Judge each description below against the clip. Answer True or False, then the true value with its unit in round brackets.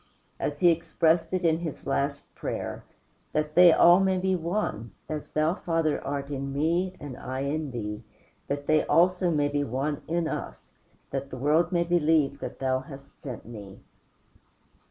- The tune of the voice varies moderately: True (3.7 semitones)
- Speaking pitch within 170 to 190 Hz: False (150 Hz)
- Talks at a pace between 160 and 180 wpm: True (170 wpm)